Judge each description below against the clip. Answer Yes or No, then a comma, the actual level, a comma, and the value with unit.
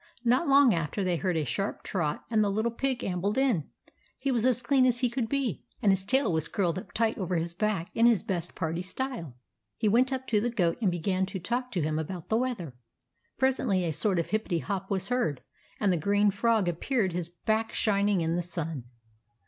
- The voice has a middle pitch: No, high, 200 Hz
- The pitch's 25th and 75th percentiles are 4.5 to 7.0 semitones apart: Yes, average, 5.3 semitones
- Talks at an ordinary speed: No, fast, 220 wpm